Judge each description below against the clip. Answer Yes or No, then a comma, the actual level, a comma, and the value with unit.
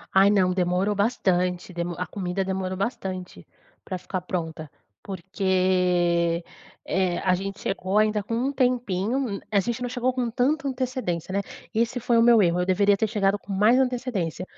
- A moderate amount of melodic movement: Yes, average, 4.3 semitones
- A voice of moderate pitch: No, high, 195 Hz